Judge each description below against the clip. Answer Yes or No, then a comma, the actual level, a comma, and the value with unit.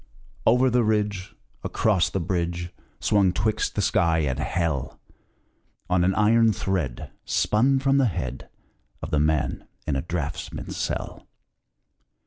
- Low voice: Yes, very low, 90 Hz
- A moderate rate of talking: No, slow, 130 wpm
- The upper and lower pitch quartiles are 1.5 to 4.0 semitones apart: No, wide, 5.4 semitones